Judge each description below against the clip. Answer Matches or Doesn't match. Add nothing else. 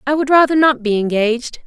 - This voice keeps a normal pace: Doesn't match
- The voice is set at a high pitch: Matches